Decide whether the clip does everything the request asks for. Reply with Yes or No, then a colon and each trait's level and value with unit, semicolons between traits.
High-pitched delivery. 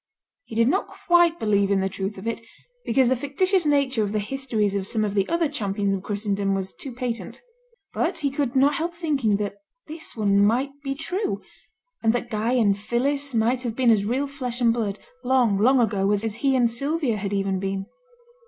Yes: high, 235 Hz